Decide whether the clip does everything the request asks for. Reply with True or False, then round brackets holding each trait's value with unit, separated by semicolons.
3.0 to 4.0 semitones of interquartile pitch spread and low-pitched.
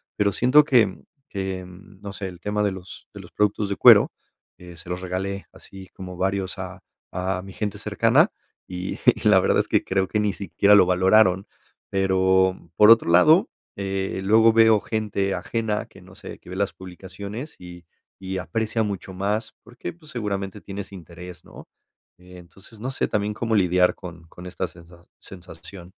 False (2.4 semitones; 95 Hz)